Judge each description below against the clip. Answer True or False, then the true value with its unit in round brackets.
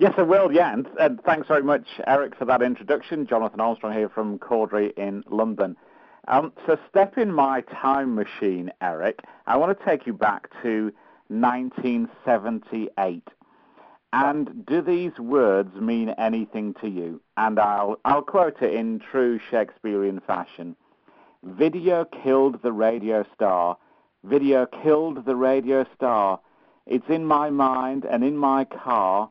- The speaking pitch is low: True (125 Hz)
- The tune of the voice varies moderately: True (4.8 semitones)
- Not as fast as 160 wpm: True (145 wpm)